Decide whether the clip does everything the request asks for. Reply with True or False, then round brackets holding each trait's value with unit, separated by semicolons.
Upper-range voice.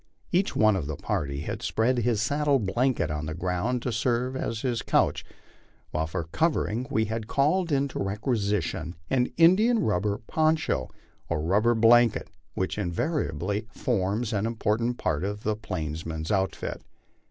False (110 Hz)